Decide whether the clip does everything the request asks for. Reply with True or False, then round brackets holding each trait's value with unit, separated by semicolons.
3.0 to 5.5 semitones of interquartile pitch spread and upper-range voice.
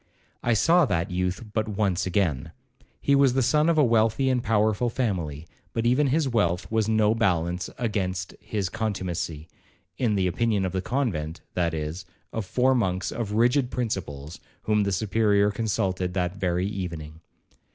False (4.5 semitones; 100 Hz)